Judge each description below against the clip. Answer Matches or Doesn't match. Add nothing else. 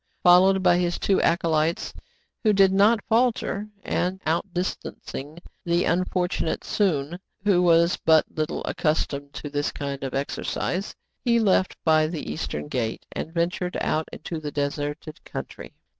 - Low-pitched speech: Doesn't match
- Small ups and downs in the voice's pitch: Doesn't match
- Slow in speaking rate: Doesn't match